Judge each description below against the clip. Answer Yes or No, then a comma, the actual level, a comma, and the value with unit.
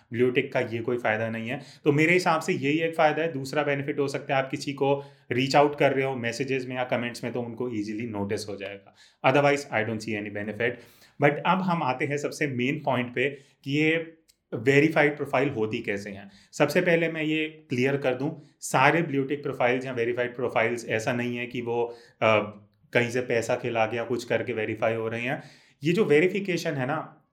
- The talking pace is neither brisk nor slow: No, fast, 210 wpm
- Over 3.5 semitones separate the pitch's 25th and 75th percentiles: Yes, average, 3.9 semitones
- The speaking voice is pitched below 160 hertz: Yes, low, 135 Hz